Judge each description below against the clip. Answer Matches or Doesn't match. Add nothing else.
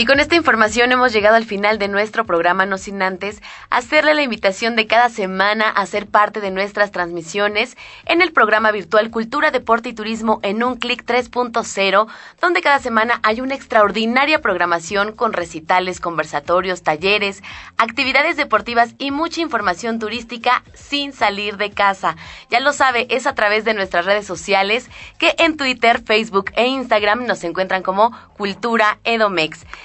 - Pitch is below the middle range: Doesn't match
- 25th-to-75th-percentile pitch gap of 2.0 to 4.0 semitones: Matches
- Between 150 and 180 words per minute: Matches